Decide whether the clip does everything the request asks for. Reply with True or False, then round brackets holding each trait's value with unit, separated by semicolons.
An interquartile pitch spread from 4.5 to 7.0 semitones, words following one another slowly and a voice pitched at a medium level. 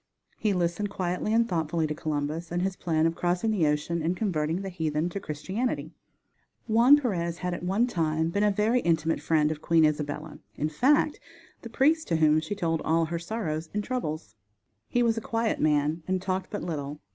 False (4.9 semitones; 195 wpm; 170 Hz)